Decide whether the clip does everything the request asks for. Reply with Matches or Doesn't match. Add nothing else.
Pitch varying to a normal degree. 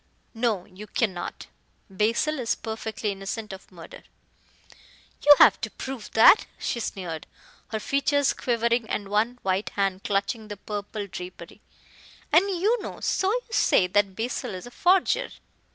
Matches